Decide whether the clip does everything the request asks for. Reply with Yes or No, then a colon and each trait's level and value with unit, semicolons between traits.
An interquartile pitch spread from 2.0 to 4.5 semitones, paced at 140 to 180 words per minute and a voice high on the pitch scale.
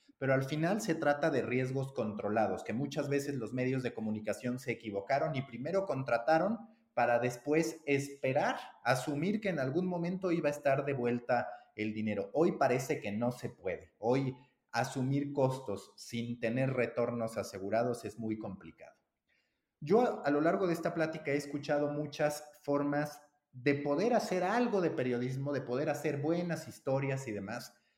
No: average, 4.1 semitones; average, 160 wpm; low, 135 Hz